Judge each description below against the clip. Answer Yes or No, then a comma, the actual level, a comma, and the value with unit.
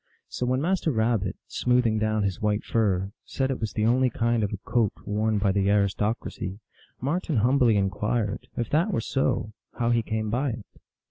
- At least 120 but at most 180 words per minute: No, average, 190 wpm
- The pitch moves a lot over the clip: No, average, 3.2 semitones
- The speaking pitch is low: Yes, low, 110 Hz